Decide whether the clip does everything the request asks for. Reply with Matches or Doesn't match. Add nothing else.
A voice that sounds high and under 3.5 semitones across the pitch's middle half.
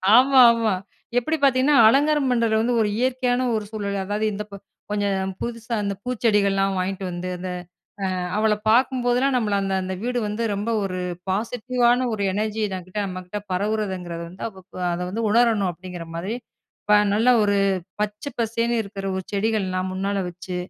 Doesn't match